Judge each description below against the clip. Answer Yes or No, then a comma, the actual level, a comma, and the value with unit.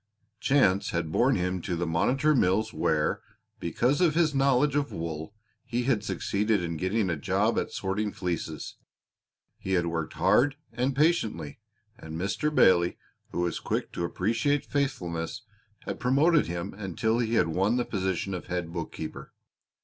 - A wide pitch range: Yes, wide, 6.9 semitones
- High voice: No, low, 100 Hz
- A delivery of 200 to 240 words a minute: No, average, 155 wpm